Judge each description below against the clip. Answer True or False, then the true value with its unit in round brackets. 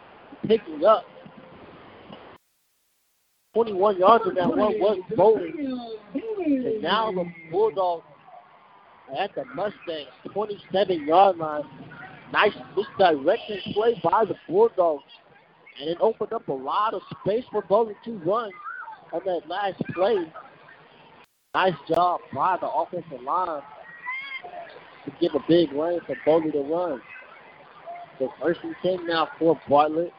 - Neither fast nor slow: False (125 wpm)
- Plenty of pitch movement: True (5.8 semitones)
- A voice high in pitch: True (200 Hz)